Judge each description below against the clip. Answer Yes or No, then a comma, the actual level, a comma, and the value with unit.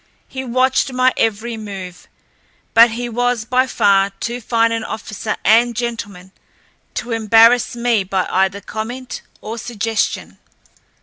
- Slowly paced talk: Yes, slow, 130 wpm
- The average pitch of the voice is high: Yes, high, 230 Hz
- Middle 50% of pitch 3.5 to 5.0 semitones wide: No, narrow, 2.5 semitones